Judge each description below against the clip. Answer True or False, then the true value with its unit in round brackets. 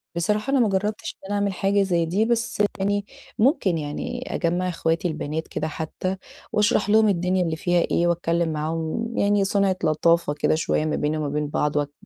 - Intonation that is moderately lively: True (4.2 semitones)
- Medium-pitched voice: True (175 Hz)